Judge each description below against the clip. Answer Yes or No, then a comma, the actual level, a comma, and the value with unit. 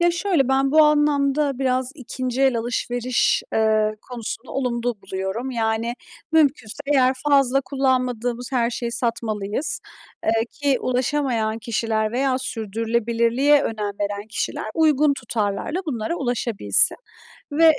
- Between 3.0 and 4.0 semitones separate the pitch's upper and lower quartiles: Yes, average, 3.4 semitones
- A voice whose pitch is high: Yes, high, 245 Hz